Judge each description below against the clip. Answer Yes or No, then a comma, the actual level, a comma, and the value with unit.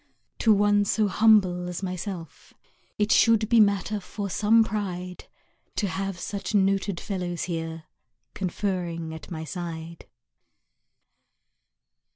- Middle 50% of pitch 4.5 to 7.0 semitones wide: No, average, 3.0 semitones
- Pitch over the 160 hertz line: Yes, high, 190 Hz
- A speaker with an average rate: No, slow, 115 wpm